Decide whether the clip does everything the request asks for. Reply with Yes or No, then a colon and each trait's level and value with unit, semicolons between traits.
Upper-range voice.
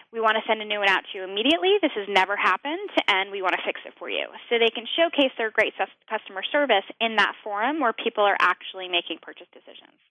Yes: high, 215 Hz